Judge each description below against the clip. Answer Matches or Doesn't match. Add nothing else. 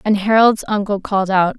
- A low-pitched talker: Doesn't match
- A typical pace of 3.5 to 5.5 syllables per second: Matches